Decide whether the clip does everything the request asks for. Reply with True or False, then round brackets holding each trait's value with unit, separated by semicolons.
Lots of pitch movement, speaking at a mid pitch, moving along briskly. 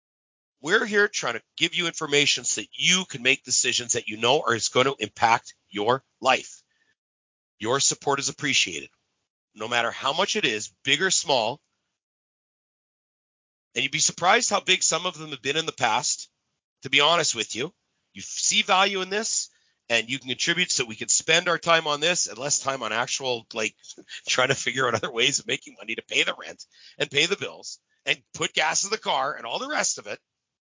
True (6.5 semitones; 145 Hz; 210 wpm)